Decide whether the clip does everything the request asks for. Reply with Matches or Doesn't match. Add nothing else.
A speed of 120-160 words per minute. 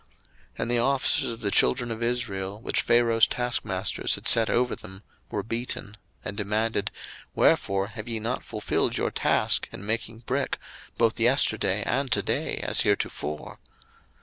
Matches